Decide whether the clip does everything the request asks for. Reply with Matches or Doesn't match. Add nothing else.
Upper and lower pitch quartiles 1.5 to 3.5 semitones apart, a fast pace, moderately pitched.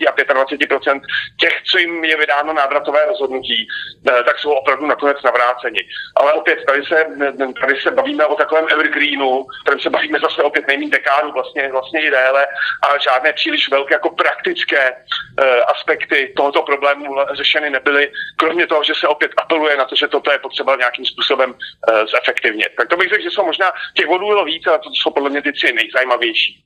Matches